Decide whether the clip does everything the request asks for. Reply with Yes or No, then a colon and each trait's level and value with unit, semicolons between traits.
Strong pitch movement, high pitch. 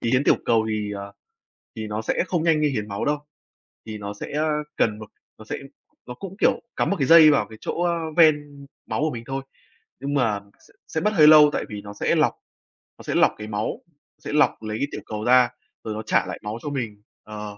No: wide, 5.9 semitones; low, 125 Hz